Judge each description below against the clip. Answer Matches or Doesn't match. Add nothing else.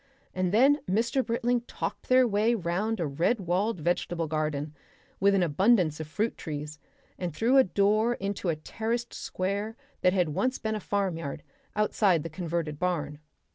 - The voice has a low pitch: Doesn't match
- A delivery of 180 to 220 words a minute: Doesn't match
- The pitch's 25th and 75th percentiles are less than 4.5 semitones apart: Doesn't match